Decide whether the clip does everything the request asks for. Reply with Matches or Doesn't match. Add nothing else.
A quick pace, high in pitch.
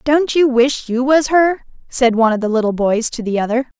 Matches